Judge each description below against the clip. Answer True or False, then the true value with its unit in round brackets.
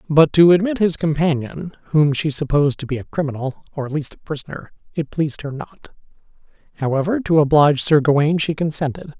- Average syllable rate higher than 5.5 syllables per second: True (5.9 syllables/s)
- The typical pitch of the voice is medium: True (150 Hz)